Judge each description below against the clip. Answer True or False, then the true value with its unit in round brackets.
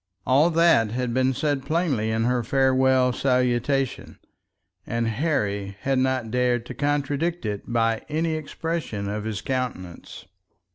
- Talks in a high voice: False (130 Hz)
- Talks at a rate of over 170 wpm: False (135 wpm)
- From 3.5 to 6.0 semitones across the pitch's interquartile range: True (4.0 semitones)